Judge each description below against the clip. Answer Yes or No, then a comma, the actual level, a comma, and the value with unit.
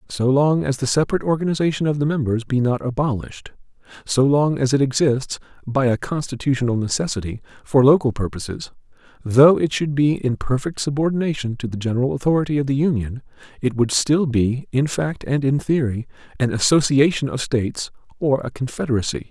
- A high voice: No, low, 135 Hz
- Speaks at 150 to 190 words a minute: Yes, average, 170 wpm